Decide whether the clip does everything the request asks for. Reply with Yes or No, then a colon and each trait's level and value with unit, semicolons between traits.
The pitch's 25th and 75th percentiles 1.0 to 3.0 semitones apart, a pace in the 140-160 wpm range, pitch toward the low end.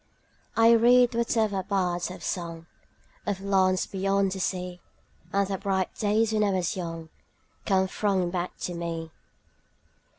No: narrow, 2.4 semitones; average, 145 wpm; high, 190 Hz